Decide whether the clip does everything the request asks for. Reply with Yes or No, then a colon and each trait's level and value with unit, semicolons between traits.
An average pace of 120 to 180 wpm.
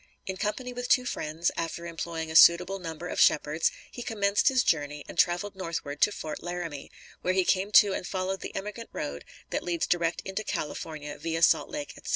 No: average, 195 wpm